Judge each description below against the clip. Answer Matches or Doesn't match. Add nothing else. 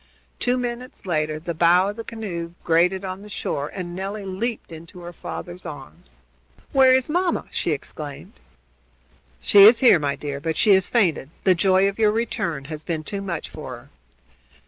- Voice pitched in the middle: Matches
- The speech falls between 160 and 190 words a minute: Matches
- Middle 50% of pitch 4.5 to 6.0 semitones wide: Matches